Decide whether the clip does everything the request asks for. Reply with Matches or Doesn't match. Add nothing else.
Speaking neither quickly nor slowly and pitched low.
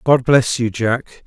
Matches